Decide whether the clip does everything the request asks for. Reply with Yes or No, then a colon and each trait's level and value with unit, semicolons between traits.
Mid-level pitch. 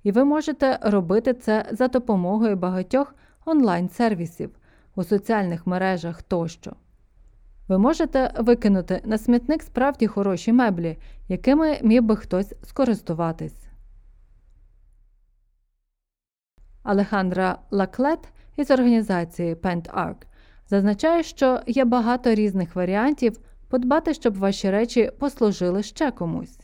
No: high, 205 Hz